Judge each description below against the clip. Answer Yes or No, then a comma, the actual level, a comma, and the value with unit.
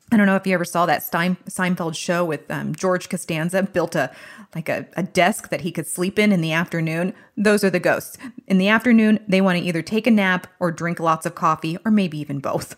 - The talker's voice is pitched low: No, medium, 180 Hz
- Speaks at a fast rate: Yes, fast, 245 wpm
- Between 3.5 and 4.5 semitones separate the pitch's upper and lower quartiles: No, average, 3.1 semitones